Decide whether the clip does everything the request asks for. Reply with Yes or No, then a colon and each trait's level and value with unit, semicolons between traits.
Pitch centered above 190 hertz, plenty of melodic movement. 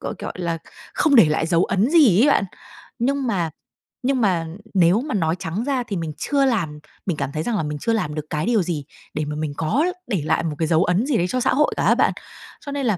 No: medium, 185 Hz; wide, 7.5 semitones